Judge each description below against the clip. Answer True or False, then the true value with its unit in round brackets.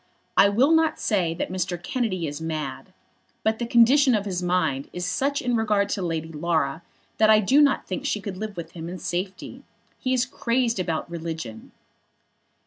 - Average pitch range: False (5.8 semitones)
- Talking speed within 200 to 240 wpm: False (185 wpm)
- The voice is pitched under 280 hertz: True (190 Hz)